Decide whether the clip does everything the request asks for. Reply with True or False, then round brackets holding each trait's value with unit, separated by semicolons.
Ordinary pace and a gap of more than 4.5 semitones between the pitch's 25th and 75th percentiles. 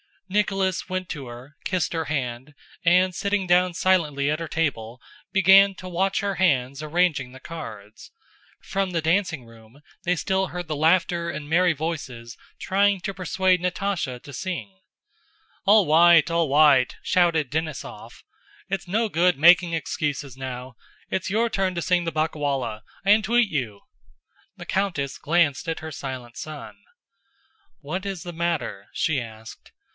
True (150 wpm; 5.1 semitones)